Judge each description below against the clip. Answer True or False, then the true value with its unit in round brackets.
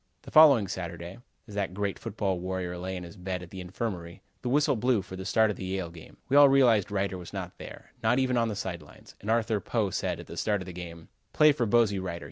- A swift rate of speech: True (255 wpm)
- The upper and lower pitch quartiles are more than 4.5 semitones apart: False (4.1 semitones)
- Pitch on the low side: True (100 Hz)